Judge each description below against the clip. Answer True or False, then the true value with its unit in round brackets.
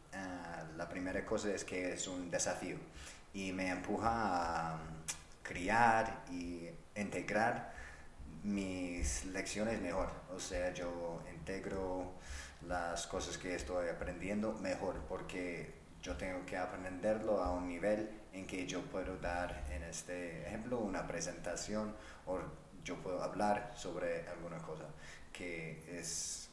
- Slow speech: True (125 wpm)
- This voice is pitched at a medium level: False (90 Hz)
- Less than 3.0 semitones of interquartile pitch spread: True (2.4 semitones)